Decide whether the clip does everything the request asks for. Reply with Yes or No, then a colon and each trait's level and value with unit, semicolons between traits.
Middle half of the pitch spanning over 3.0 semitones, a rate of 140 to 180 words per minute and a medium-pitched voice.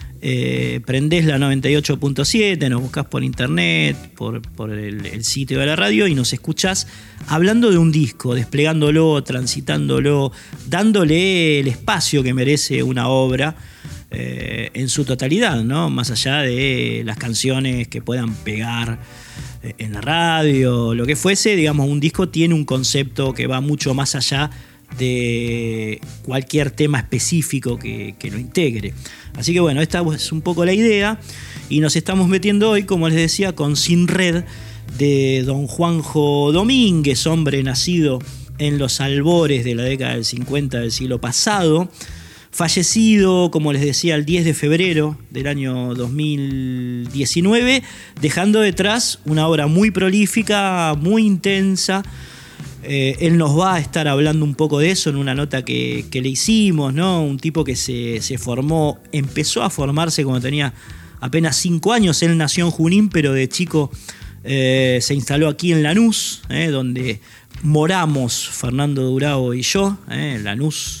Yes: average, 4.7 semitones; average, 155 wpm; medium, 145 Hz